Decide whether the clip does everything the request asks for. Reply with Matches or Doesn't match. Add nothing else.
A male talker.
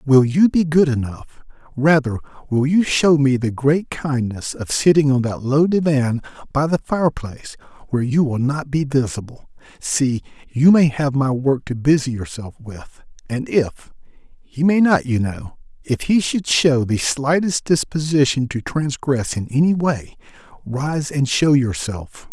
Matches